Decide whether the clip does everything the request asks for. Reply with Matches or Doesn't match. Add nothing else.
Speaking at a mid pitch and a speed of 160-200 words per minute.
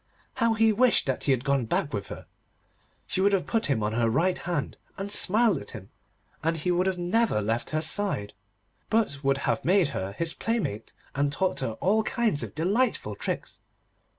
Matches